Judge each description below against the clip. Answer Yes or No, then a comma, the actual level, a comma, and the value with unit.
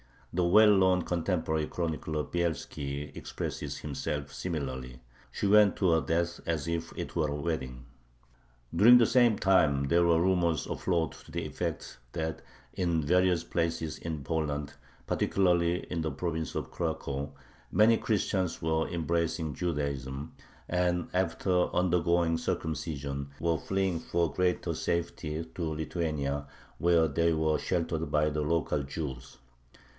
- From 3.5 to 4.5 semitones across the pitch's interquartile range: No, average, 2.7 semitones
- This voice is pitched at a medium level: No, very low, 80 Hz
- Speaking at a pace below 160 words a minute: Yes, slow, 135 wpm